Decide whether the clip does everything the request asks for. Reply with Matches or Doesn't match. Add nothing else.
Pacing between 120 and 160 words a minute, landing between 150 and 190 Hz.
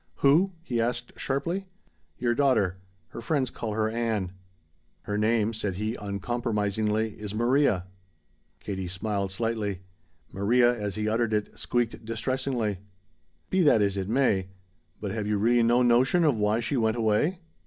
Doesn't match